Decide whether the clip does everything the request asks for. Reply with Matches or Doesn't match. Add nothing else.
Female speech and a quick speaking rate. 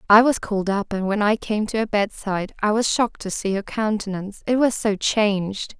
Matches